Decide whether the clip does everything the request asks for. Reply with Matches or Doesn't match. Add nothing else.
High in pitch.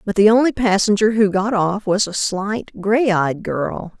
Matches